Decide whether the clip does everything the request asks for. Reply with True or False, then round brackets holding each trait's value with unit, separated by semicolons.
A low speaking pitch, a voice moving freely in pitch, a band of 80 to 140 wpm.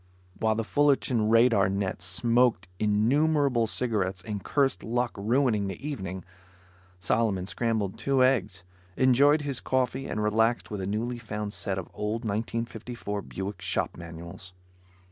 False (110 Hz; 4.0 semitones; 135 wpm)